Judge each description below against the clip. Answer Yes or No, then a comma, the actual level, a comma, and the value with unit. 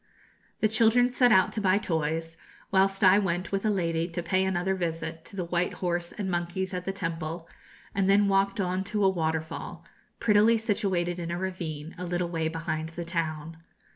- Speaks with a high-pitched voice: No, medium, 180 Hz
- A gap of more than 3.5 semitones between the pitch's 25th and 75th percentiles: No, average, 2.9 semitones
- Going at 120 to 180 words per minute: No, average, 190 wpm